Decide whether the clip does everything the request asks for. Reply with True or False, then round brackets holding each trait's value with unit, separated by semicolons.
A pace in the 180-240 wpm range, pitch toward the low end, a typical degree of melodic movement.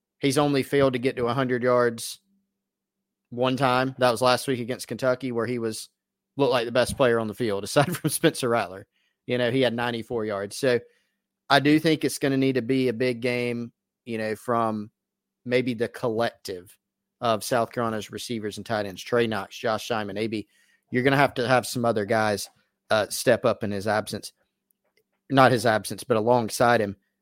True (195 wpm; 120 Hz; 3.0 semitones)